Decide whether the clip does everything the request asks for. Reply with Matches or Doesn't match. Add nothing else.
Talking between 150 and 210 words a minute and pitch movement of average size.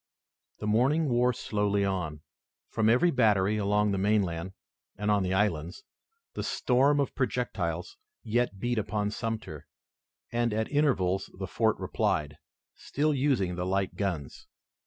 Doesn't match